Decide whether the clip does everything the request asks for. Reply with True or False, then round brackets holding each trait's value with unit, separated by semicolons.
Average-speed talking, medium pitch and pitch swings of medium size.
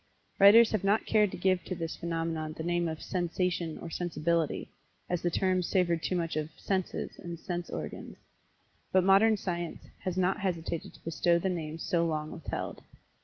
False (175 wpm; 175 Hz; 2.2 semitones)